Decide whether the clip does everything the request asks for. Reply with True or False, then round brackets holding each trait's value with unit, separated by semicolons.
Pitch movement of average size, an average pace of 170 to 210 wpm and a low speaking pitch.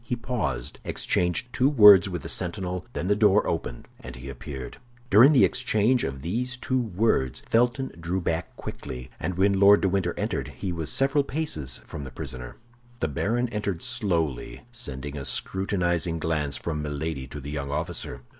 False (7.2 semitones; 175 wpm; 90 Hz)